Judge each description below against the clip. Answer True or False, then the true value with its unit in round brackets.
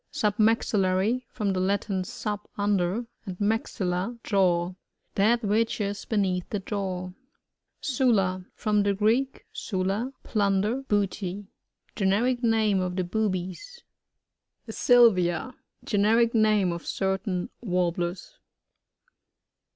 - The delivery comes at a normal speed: False (110 wpm)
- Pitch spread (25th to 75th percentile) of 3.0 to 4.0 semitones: True (3.3 semitones)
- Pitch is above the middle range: True (205 Hz)